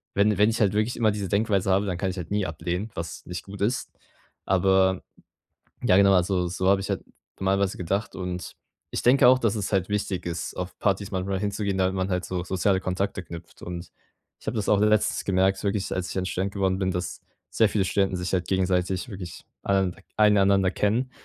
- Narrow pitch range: Yes, narrow, 1.9 semitones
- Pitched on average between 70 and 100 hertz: Yes, very low, 95 Hz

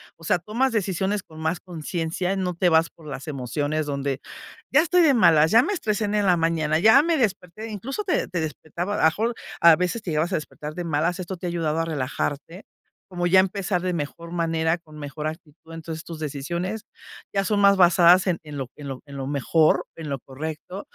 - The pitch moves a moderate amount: Yes, average, 3.7 semitones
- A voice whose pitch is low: No, medium, 170 Hz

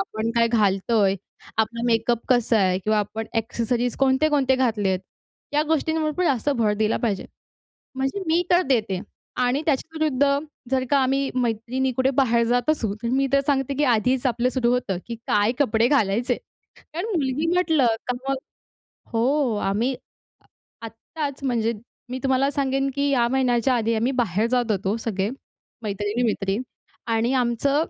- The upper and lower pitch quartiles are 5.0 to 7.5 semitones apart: No, average, 3.4 semitones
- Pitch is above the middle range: Yes, high, 245 Hz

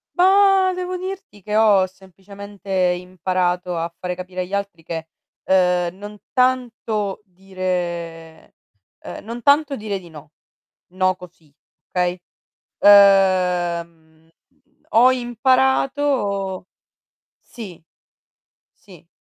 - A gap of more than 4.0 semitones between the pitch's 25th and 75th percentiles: Yes, average, 4.4 semitones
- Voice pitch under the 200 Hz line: Yes, high, 190 Hz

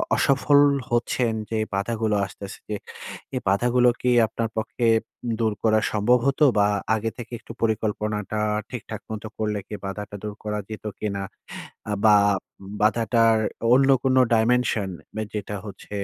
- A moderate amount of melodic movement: No, narrow, 2.3 semitones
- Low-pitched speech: Yes, low, 110 Hz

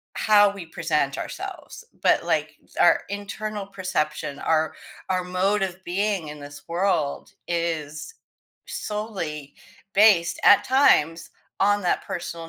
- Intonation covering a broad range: No, average, 4.1 semitones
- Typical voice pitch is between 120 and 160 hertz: No, medium, 185 Hz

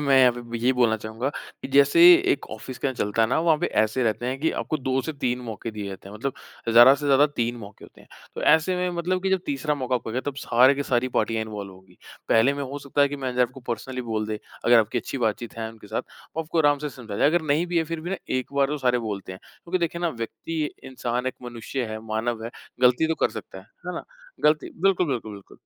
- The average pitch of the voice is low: Yes, low, 130 Hz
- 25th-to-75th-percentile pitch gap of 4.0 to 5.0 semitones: Yes, average, 4.3 semitones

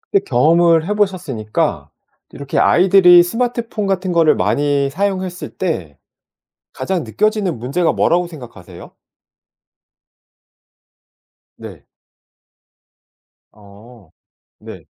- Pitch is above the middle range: No, medium, 170 Hz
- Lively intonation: Yes, wide, 6.8 semitones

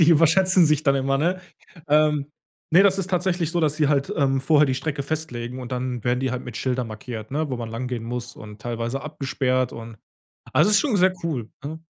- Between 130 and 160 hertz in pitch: Yes, medium, 140 Hz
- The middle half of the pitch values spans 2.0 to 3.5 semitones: No, average, 4.3 semitones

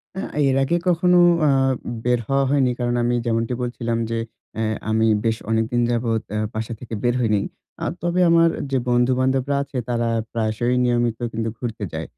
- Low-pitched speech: Yes, low, 120 Hz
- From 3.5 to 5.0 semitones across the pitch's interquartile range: No, narrow, 2.6 semitones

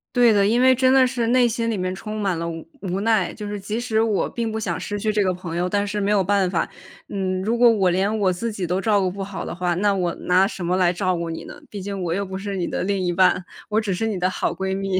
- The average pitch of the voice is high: Yes, high, 195 Hz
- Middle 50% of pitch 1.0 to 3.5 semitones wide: Yes, average, 2.9 semitones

